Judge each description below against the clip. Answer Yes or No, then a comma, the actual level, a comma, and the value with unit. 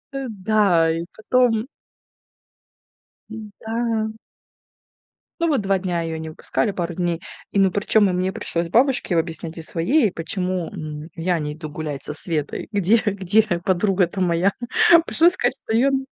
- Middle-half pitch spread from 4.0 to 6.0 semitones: Yes, average, 4.7 semitones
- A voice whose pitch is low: No, medium, 185 Hz